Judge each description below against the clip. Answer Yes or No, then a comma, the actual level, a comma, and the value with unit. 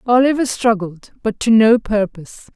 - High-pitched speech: Yes, high, 220 Hz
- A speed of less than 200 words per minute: Yes, average, 140 wpm